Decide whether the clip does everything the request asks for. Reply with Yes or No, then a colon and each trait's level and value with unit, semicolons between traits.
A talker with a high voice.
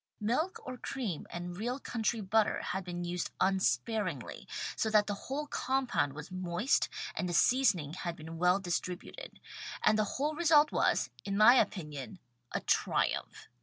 Yes: high, 195 Hz